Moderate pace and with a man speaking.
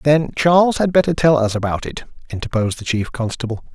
Yes: average, 190 wpm; male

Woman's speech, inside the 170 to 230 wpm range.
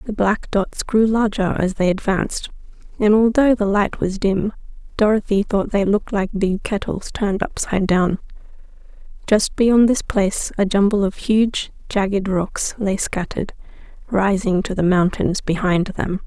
No: female; average, 155 wpm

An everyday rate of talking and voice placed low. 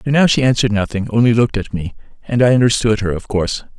No: fast, 240 wpm; low, 115 Hz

